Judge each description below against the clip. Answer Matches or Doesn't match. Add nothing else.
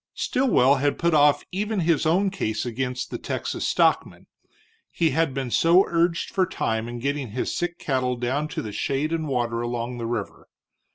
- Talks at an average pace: Matches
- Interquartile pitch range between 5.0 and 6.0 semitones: Matches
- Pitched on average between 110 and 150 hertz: Matches